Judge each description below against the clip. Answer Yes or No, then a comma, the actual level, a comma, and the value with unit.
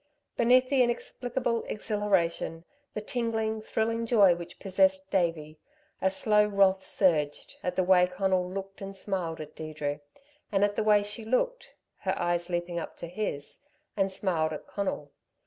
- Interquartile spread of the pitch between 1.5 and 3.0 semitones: No, average, 3.7 semitones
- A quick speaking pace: No, average, 155 wpm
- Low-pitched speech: No, high, 190 Hz